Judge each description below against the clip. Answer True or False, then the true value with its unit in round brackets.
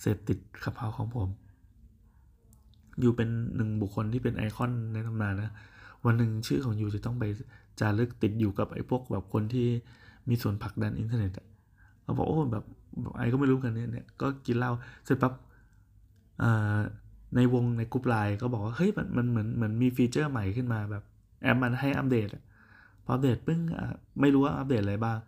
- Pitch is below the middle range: True (115 Hz)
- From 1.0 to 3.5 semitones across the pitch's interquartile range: True (2.9 semitones)